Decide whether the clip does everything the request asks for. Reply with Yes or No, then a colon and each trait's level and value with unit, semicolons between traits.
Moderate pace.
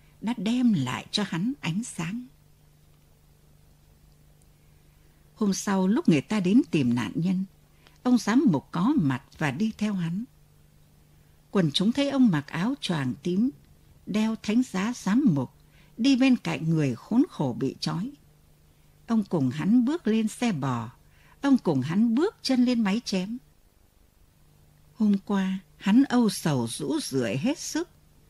No: slow, 150 wpm